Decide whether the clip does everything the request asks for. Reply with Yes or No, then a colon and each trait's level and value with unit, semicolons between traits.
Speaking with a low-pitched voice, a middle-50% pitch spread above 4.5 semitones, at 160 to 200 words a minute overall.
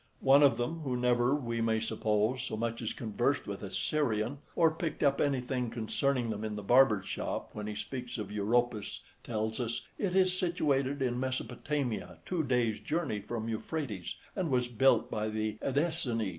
No: low, 120 Hz; average, 4.2 semitones; average, 175 wpm